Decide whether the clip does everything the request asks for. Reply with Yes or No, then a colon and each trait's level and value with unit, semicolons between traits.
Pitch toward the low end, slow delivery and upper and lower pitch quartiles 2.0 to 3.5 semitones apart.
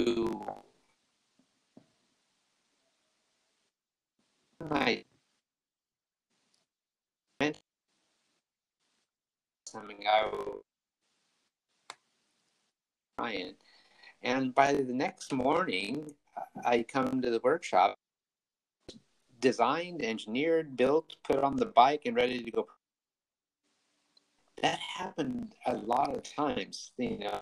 No: low, 130 Hz; slow, 65 wpm; average, 4.7 semitones